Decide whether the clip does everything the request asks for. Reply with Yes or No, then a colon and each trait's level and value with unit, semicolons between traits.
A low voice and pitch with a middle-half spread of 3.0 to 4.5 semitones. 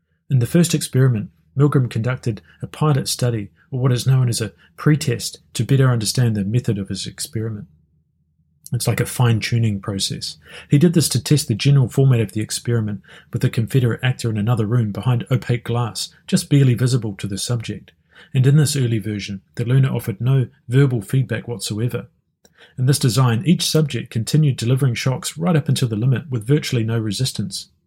Yes: low, 120 Hz; average, 3.3 semitones